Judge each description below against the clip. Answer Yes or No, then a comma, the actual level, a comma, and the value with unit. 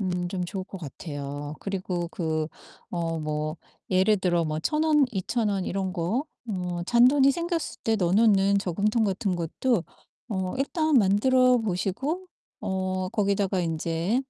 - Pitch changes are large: No, average, 4.6 semitones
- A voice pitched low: No, high, 190 Hz